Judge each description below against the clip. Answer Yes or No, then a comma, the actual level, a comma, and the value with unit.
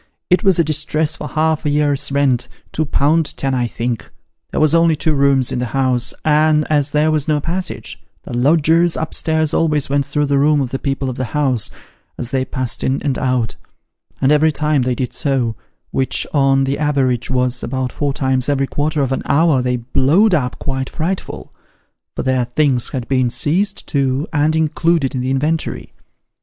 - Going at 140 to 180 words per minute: No, average, 195 wpm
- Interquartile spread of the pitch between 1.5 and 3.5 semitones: Yes, average, 3.0 semitones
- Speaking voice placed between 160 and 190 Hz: No, medium, 140 Hz